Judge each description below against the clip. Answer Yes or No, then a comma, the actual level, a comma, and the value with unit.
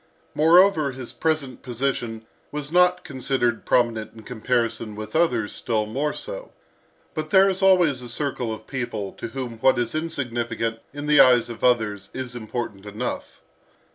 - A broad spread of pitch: No, average, 4.6 semitones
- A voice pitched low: Yes, low, 125 Hz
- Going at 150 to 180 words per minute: Yes, average, 155 wpm